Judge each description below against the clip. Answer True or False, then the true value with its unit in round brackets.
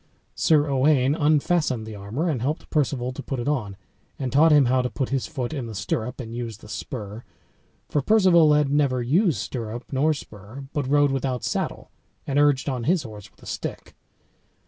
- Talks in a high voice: False (135 Hz)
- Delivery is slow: False (190 wpm)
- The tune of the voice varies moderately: True (3.8 semitones)